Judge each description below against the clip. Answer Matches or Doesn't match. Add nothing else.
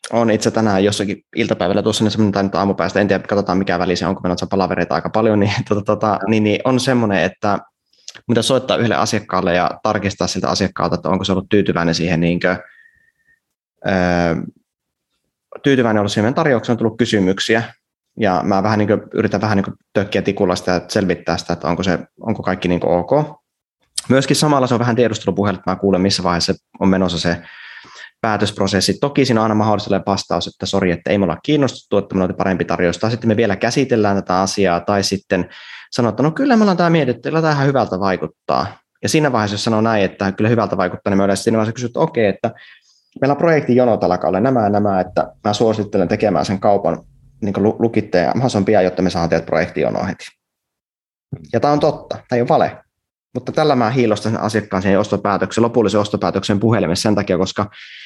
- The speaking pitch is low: Matches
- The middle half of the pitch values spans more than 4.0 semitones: Doesn't match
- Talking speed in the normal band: Doesn't match